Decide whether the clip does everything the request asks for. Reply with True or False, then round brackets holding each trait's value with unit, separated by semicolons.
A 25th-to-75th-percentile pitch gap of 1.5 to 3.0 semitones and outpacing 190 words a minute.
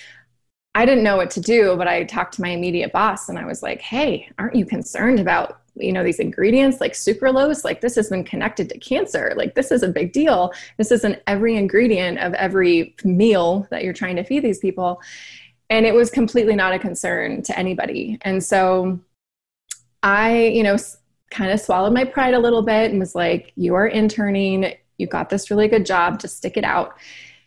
False (3.7 semitones; 205 wpm)